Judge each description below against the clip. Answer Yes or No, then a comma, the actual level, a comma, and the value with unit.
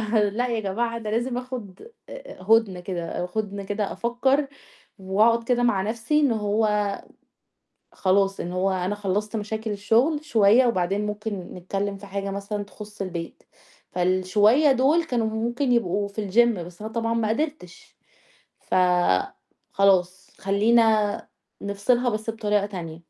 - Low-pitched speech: No, high, 210 Hz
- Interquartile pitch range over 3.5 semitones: No, average, 3.1 semitones